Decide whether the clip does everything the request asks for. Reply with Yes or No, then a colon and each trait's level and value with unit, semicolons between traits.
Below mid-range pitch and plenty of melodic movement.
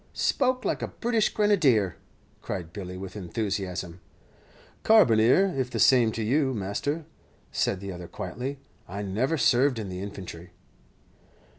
Yes: low, 110 Hz; wide, 6.9 semitones